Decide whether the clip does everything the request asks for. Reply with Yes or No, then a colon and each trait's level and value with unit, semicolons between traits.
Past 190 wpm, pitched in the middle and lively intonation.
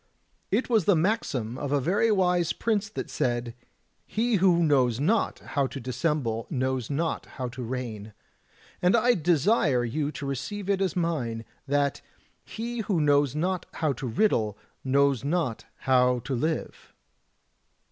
No: average, 150 wpm; medium, 145 Hz; wide, 6.4 semitones